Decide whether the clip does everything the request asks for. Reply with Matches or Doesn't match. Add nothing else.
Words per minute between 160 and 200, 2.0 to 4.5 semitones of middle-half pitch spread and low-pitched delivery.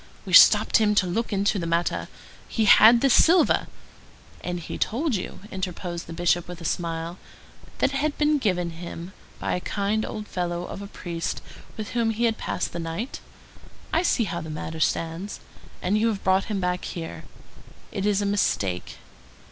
Doesn't match